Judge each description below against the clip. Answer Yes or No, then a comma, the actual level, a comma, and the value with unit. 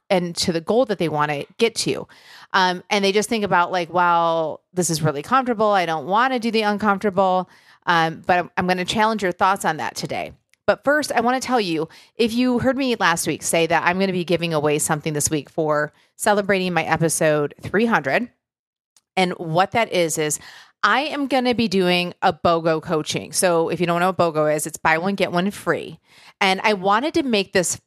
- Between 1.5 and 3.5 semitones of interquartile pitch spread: No, average, 4.2 semitones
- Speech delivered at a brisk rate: Yes, fast, 225 wpm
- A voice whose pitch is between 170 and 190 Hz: Yes, medium, 185 Hz